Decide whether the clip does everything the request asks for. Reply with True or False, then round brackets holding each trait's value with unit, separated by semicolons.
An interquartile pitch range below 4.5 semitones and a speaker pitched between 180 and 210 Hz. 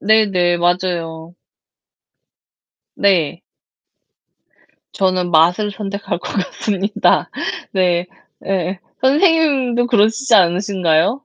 True (3.7 semitones; 190 Hz)